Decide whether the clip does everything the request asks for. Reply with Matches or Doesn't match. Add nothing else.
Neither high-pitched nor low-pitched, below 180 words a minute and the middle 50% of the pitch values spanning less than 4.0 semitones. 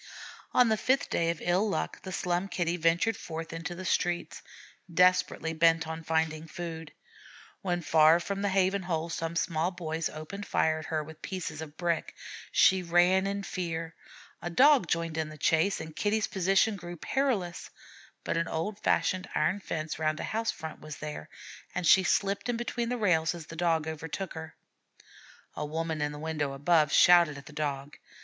Doesn't match